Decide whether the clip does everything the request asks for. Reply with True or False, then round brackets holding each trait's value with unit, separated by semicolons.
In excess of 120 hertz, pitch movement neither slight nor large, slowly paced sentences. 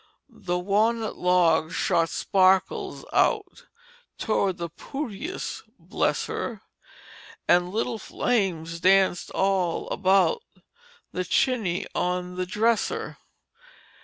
True (190 Hz; 3.6 semitones; 95 wpm)